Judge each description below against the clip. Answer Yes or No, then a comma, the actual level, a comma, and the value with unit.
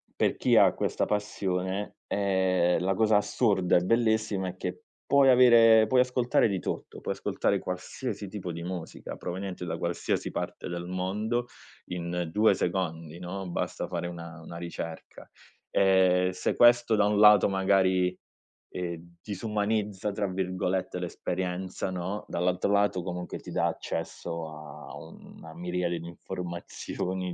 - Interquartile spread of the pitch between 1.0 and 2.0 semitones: No, average, 2.7 semitones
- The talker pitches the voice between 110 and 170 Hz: No, very low, 95 Hz